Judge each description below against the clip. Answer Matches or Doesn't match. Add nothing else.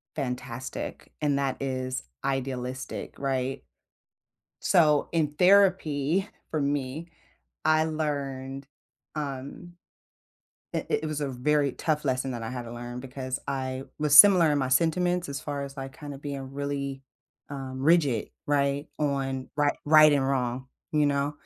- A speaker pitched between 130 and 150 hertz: Matches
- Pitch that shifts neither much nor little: Doesn't match